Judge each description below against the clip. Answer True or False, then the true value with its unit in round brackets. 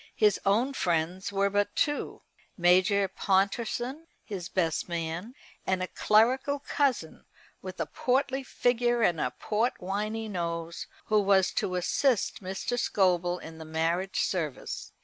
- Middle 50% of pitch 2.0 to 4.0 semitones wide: False (4.8 semitones)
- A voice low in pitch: False (195 Hz)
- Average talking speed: False (130 wpm)